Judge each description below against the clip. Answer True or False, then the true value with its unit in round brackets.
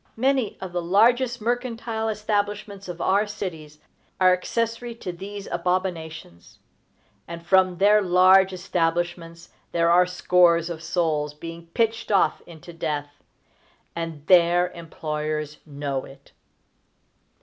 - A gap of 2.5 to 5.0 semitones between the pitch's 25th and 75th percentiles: True (3.6 semitones)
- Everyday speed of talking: False (115 wpm)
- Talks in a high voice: False (180 Hz)